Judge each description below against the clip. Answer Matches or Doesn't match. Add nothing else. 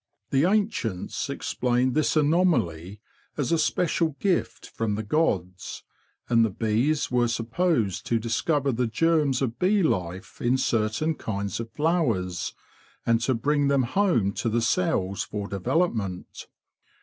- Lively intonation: Matches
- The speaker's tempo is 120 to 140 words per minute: Matches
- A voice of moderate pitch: Doesn't match